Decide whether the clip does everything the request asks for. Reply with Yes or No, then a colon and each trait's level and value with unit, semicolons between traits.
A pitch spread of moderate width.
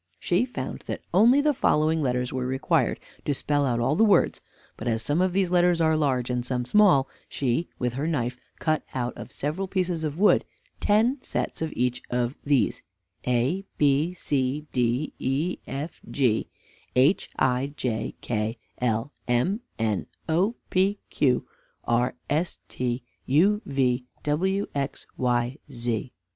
No: wide, 5.8 semitones